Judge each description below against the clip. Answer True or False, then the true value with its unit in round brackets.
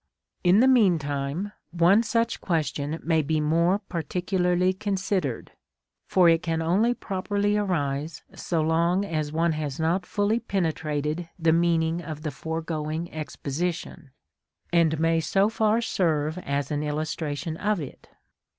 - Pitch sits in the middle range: True (165 Hz)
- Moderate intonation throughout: True (3.4 semitones)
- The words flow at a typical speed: False (130 wpm)